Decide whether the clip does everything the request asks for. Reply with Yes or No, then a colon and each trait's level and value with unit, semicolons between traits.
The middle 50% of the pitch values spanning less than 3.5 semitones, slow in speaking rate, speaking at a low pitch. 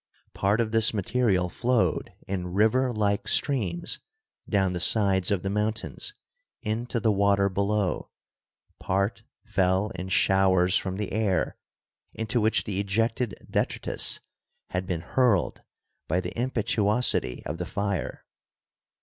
Yes: average, 2.9 semitones; slow, 125 wpm; low, 100 Hz